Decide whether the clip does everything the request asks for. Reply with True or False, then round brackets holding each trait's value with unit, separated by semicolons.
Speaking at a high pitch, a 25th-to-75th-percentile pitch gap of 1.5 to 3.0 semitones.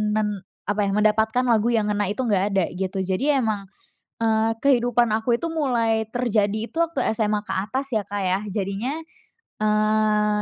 True (215 Hz; 2.6 semitones)